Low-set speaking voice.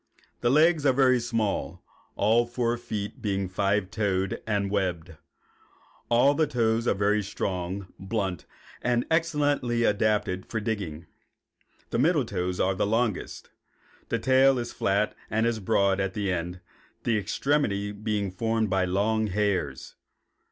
Yes: low, 105 Hz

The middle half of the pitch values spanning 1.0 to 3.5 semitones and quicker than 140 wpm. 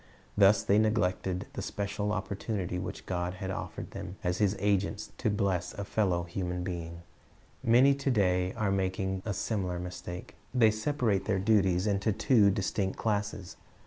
Yes: narrow, 2.6 semitones; average, 150 wpm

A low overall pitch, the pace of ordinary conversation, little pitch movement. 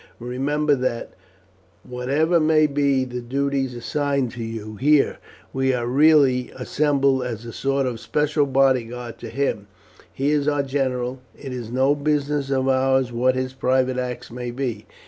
Yes: low, 130 Hz; average, 155 wpm; narrow, 2.2 semitones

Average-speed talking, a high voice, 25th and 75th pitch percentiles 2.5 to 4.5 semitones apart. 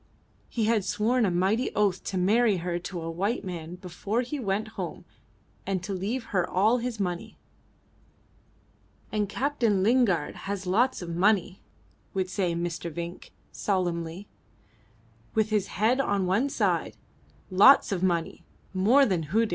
Yes: average, 145 wpm; high, 195 Hz; average, 3.8 semitones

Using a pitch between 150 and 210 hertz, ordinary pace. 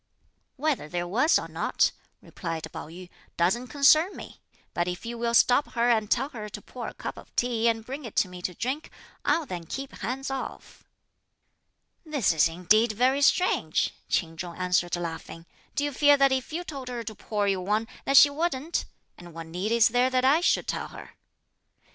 No: high, 235 Hz; average, 195 wpm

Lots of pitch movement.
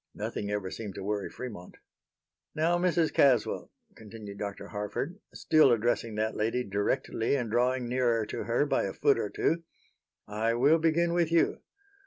Yes: wide, 6.5 semitones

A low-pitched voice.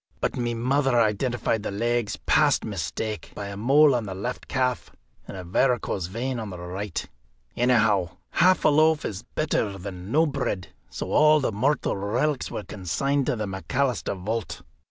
Yes: low, 115 Hz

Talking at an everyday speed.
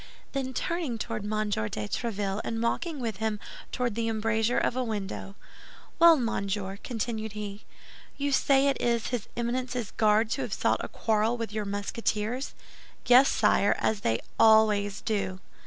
Yes: average, 155 wpm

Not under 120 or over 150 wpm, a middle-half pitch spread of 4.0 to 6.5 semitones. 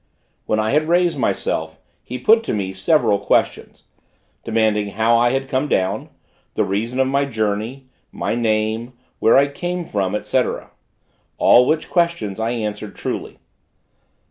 Yes: average, 145 wpm; average, 4.7 semitones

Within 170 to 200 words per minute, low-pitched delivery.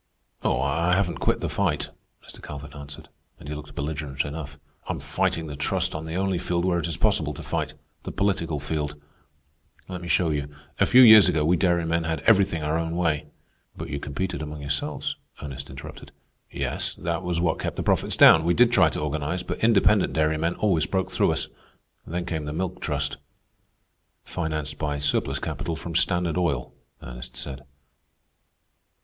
Yes: average, 180 wpm; very low, 80 Hz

